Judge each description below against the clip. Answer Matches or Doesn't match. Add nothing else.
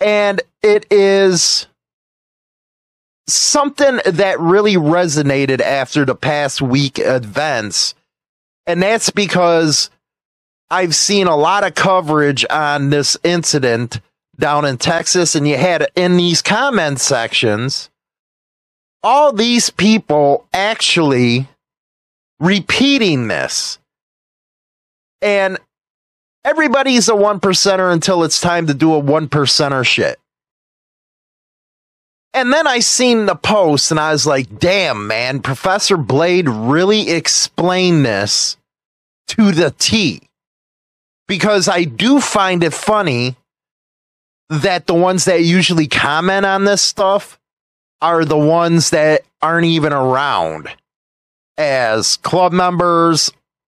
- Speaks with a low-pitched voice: Doesn't match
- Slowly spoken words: Matches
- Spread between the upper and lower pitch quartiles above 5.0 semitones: Matches